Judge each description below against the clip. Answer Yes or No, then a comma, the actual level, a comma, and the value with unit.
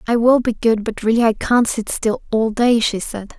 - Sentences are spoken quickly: Yes, fast, 250 wpm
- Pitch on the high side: Yes, high, 225 Hz